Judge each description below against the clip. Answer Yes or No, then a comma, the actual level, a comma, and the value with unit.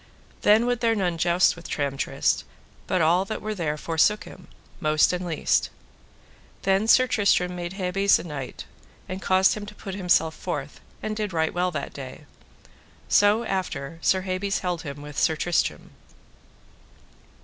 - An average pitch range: Yes, average, 4.0 semitones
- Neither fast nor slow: Yes, average, 160 wpm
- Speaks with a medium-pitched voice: Yes, medium, 180 Hz